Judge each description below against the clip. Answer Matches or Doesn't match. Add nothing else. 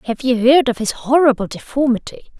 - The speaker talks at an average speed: Matches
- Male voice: Doesn't match